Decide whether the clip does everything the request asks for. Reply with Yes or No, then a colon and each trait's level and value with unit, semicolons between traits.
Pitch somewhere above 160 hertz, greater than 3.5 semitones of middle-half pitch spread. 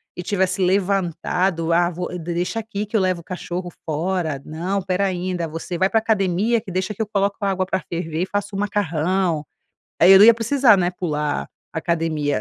No: medium, 185 Hz; average, 2.7 semitones